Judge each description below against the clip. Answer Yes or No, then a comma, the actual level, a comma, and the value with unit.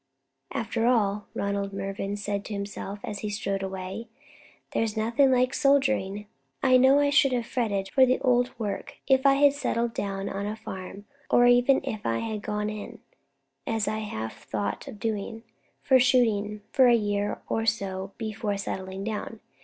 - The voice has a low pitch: No, high, 215 Hz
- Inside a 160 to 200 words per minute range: Yes, average, 170 wpm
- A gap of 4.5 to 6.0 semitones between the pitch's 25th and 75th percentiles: No, average, 3.5 semitones